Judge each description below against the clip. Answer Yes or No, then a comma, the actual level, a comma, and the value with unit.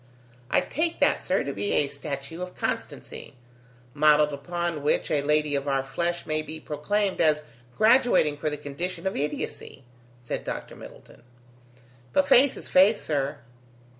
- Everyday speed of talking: Yes, average, 155 wpm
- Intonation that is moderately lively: Yes, average, 4.1 semitones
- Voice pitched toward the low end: No, medium, 155 Hz